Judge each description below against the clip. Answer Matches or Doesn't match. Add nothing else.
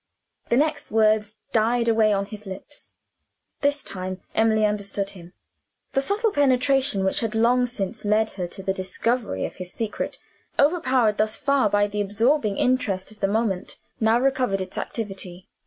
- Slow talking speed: Doesn't match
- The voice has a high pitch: Matches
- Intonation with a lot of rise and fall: Doesn't match